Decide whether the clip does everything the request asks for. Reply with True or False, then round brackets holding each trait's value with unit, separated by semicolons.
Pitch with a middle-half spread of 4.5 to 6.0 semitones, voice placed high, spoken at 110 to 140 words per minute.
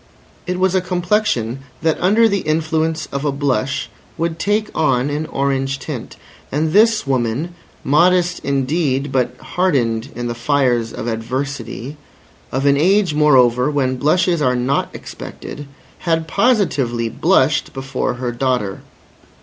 False (4.9 semitones; 140 Hz; 135 wpm)